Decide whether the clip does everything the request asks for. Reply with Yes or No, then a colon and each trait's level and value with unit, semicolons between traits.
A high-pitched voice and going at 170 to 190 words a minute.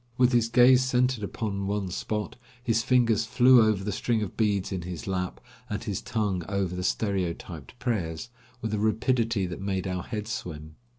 No: low, 105 Hz; average, 180 wpm